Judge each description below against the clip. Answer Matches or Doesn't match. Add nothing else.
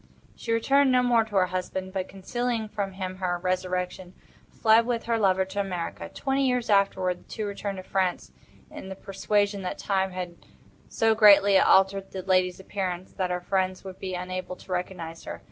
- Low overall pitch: Doesn't match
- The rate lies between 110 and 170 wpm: Doesn't match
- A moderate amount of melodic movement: Doesn't match